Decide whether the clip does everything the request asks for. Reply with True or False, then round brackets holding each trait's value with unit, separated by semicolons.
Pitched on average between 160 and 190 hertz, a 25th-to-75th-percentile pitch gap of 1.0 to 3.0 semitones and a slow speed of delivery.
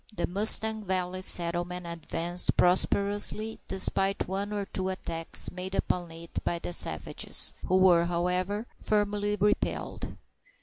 True (185 Hz; 2.7 semitones; 125 wpm)